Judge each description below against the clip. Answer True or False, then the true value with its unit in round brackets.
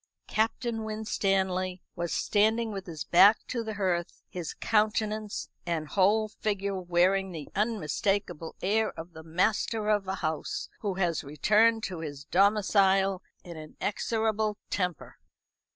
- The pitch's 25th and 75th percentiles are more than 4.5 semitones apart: False (3.5 semitones)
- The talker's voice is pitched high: True (195 Hz)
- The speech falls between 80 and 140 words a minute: True (135 wpm)